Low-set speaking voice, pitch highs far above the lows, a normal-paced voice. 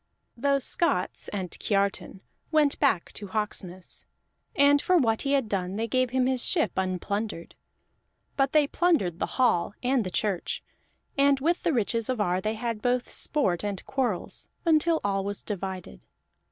No: high, 225 Hz; wide, 6.1 semitones; average, 160 wpm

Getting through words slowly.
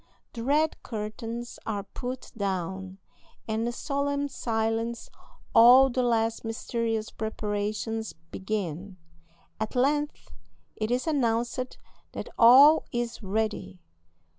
Yes: slow, 105 wpm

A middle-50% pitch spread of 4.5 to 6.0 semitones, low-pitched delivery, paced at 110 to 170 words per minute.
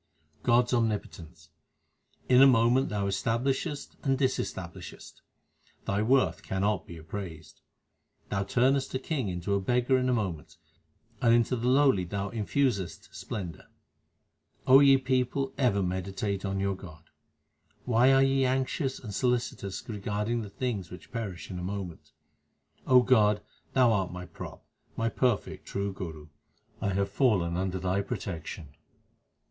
Yes: average, 5.1 semitones; low, 105 Hz; average, 140 wpm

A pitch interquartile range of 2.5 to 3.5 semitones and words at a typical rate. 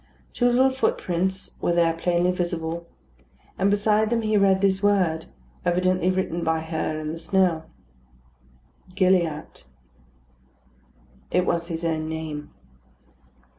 No: average, 2.8 semitones; slow, 120 wpm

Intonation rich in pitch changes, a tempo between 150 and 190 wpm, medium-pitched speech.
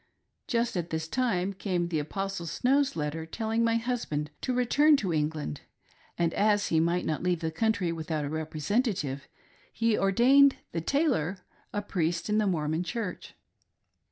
Yes: wide, 6.1 semitones; average, 155 wpm; medium, 180 Hz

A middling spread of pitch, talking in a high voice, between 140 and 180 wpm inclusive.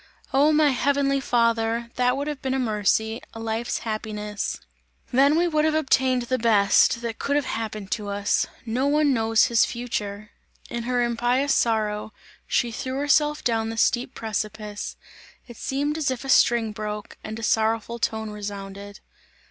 Yes: average, 3.6 semitones; high, 235 Hz; average, 165 wpm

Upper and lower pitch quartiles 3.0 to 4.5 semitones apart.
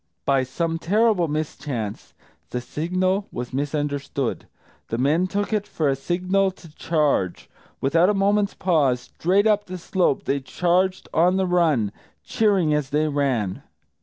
No: average, 5.2 semitones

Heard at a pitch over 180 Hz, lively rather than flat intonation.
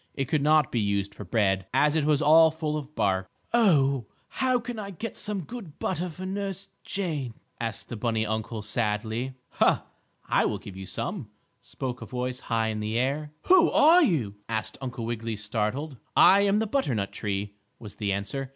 No: low, 130 Hz; wide, 7.2 semitones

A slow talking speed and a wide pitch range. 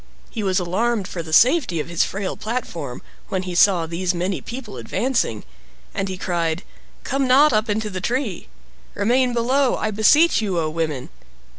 No: average, 170 wpm; wide, 5.7 semitones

